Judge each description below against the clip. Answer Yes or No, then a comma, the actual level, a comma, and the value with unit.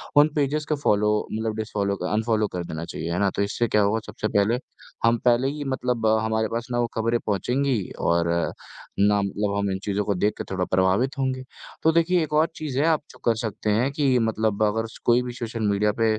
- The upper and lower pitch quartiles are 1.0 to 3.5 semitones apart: No, average, 3.9 semitones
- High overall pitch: No, low, 110 Hz